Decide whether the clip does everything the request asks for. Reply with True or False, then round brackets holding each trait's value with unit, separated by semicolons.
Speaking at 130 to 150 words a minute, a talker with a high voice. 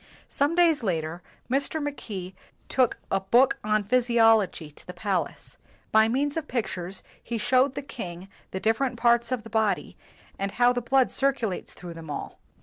False (170 wpm; 225 Hz)